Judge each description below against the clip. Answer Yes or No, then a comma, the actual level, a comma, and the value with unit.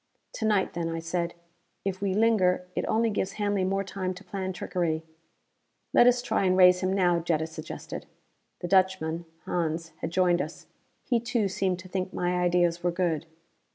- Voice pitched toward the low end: No, medium, 185 Hz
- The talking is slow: No, average, 180 wpm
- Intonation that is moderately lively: No, narrow, 2.2 semitones